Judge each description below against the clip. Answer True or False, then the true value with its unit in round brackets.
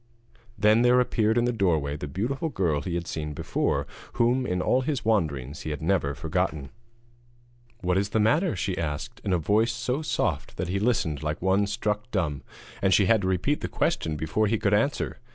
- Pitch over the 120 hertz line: False (100 Hz)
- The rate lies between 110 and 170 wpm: False (200 wpm)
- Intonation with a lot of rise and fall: True (6.6 semitones)